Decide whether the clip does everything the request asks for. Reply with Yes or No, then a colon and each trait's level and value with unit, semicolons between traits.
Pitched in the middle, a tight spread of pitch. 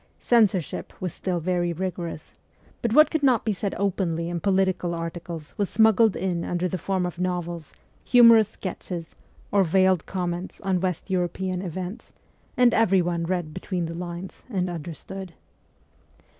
Yes: medium, 180 Hz; narrow, 2.2 semitones